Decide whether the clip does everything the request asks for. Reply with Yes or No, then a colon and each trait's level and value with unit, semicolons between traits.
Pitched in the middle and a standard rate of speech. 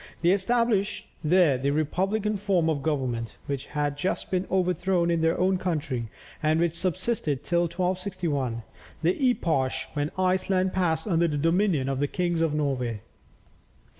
Yes: medium, 170 Hz; average, 150 wpm